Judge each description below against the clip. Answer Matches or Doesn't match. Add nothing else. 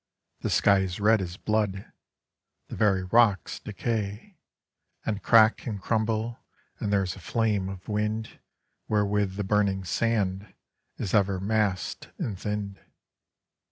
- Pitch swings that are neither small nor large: Doesn't match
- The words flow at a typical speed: Doesn't match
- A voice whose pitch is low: Matches